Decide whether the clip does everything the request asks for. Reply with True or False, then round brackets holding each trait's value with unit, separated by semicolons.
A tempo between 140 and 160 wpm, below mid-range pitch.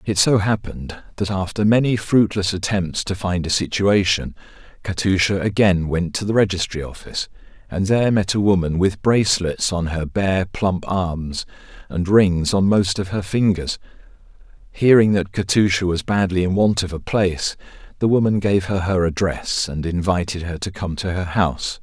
False (170 wpm; 95 Hz)